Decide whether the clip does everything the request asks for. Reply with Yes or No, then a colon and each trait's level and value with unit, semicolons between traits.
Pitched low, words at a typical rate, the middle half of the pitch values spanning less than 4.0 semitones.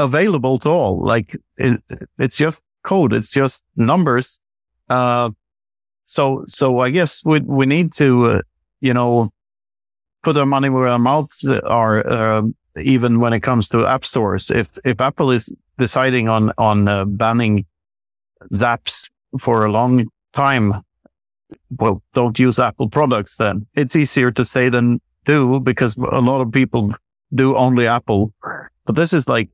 Yes: low, 125 Hz; average, 155 wpm; average, 3.6 semitones